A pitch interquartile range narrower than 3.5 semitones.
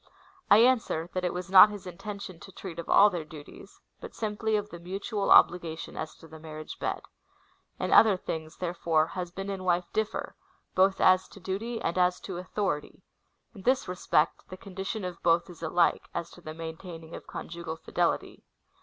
Yes: average, 3.0 semitones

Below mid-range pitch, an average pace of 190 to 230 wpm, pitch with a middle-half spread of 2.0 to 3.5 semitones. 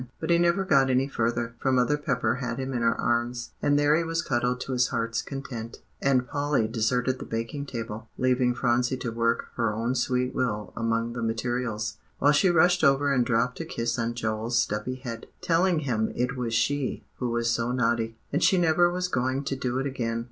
Yes: low, 125 Hz; fast, 205 wpm; average, 3.1 semitones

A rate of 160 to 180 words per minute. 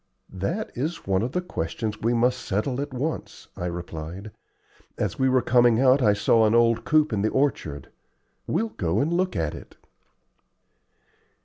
Yes: average, 170 wpm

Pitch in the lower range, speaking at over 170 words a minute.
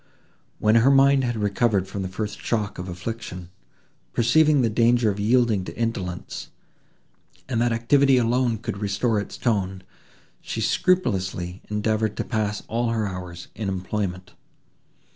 No: low, 110 Hz; average, 145 wpm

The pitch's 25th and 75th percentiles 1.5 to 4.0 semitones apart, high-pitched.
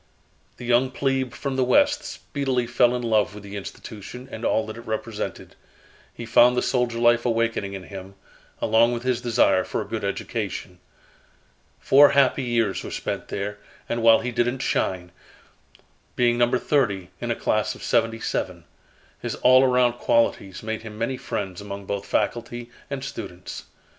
No: average, 3.1 semitones; low, 120 Hz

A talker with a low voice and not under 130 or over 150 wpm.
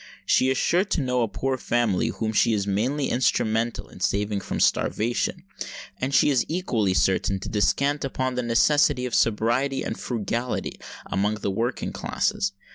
No: low, 120 Hz; average, 165 wpm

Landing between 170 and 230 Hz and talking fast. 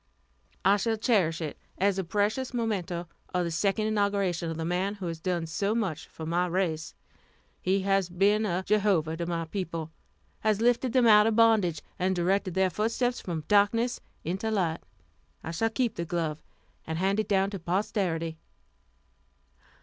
No: high, 190 Hz; average, 170 wpm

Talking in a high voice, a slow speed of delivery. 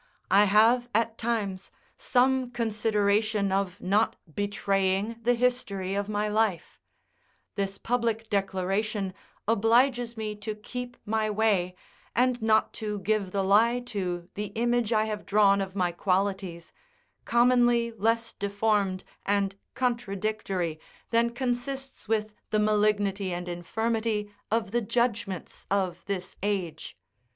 Yes: high, 210 Hz; slow, 125 wpm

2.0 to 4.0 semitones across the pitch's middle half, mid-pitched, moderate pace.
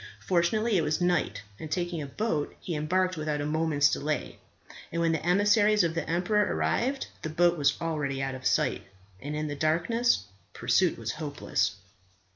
Yes: average, 3.6 semitones; medium, 165 Hz; average, 175 wpm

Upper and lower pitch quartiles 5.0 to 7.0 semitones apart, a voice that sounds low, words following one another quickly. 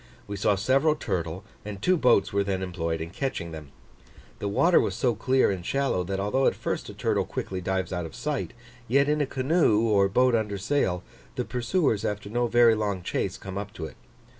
Yes: wide, 5.5 semitones; low, 105 Hz; fast, 210 wpm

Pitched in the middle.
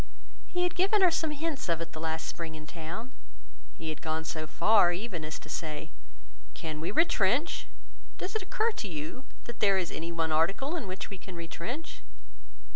Yes: medium, 180 Hz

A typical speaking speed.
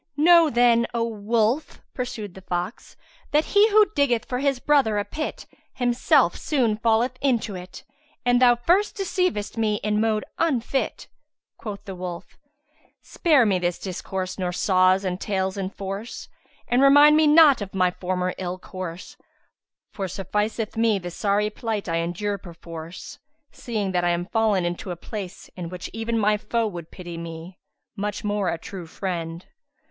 Yes: average, 160 wpm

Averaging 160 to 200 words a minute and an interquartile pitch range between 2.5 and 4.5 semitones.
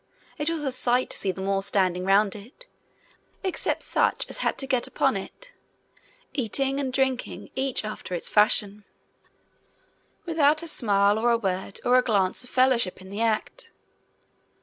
No: average, 165 wpm; average, 5.2 semitones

